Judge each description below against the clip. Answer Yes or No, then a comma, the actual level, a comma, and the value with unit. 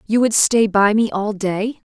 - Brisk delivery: Yes, fast, 220 wpm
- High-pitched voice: Yes, high, 210 Hz